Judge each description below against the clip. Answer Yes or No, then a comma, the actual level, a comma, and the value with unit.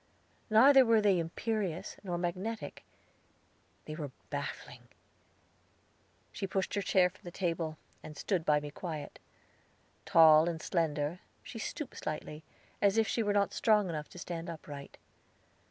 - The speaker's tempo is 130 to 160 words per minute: Yes, average, 140 wpm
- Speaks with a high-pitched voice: No, medium, 175 Hz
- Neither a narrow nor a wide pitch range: Yes, average, 4.5 semitones